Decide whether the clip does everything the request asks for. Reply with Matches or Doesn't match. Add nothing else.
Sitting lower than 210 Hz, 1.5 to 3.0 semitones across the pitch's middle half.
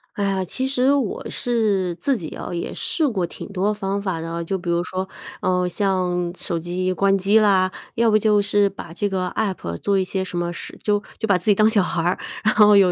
Matches